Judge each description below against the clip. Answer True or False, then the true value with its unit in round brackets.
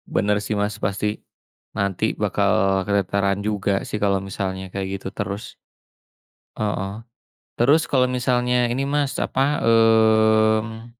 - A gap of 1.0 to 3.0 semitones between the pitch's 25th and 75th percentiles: True (2.5 semitones)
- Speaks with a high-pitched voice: False (110 Hz)